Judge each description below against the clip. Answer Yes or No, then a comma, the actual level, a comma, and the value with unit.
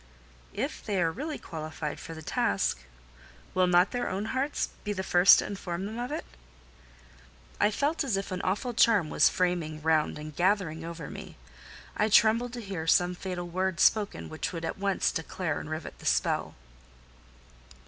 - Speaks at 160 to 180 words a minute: Yes, average, 175 wpm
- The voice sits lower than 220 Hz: Yes, medium, 185 Hz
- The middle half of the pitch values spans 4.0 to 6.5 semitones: Yes, average, 4.3 semitones